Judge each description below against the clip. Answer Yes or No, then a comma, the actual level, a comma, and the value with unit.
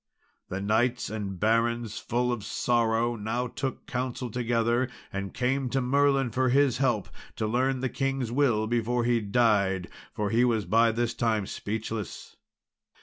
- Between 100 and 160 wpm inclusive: Yes, average, 150 wpm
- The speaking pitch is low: Yes, low, 120 Hz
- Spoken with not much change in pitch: Yes, narrow, 2.3 semitones